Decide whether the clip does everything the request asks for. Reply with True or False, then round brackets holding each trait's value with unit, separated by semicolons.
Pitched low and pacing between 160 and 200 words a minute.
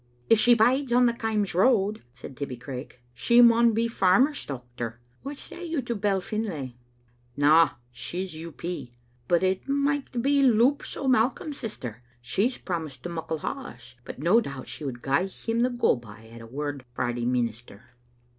False (185 Hz; 185 wpm)